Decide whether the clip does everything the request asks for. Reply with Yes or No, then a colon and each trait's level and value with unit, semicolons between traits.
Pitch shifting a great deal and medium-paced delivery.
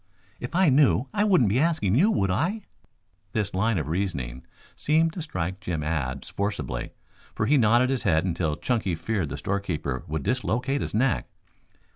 Yes: wide, 8.6 semitones; average, 170 wpm